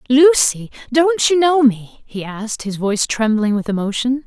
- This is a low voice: No, high, 245 Hz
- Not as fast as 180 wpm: Yes, average, 170 wpm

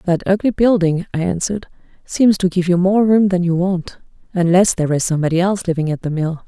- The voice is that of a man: No, female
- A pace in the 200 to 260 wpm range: Yes, fast, 205 wpm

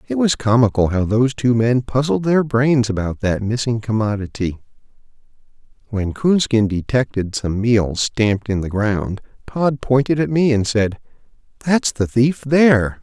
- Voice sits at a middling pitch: No, low, 120 Hz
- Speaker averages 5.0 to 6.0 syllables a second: No, 4.5 syllables/s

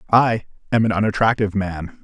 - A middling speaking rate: Yes, average, 150 wpm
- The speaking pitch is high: No, low, 105 Hz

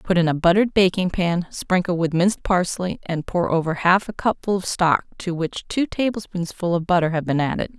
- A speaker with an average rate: No, fast, 210 wpm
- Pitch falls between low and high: Yes, medium, 180 Hz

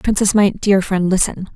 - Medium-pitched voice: No, high, 195 Hz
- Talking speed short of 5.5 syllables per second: Yes, 4.7 syllables/s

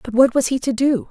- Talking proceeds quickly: Yes, fast, 325 wpm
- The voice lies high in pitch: Yes, very high, 255 Hz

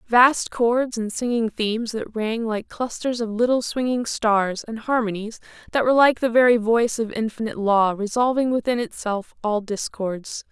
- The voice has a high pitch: Yes, high, 225 Hz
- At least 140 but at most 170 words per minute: Yes, average, 165 wpm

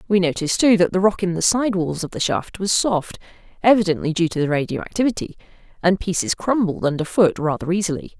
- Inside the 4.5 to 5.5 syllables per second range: No, 5.9 syllables/s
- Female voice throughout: Yes, female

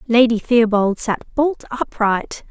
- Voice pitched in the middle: No, high, 235 Hz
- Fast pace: No, slow, 120 wpm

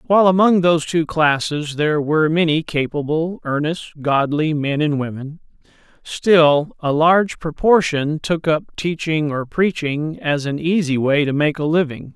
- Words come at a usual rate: Yes, average, 155 wpm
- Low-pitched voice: No, medium, 155 Hz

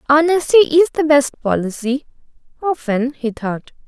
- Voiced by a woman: Yes, female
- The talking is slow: Yes, slow, 110 wpm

